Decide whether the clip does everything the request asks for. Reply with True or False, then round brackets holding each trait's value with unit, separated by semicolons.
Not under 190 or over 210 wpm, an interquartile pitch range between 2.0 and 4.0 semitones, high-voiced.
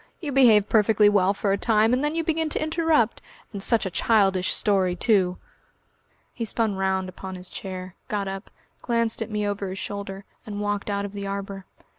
True (195 wpm; 2.8 semitones; 205 Hz)